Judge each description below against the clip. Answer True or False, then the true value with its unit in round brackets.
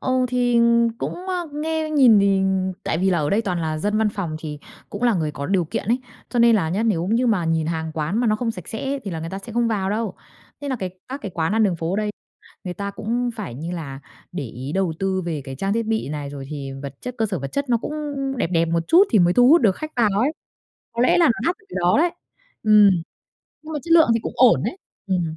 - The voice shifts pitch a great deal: True (6.4 semitones)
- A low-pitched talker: False (200 Hz)